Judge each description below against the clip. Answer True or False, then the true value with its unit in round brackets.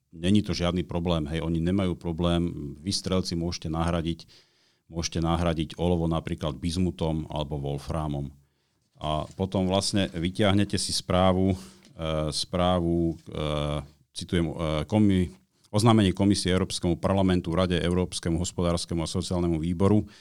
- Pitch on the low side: True (85 Hz)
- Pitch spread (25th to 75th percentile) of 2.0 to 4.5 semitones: True (2.5 semitones)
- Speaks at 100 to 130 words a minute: True (115 wpm)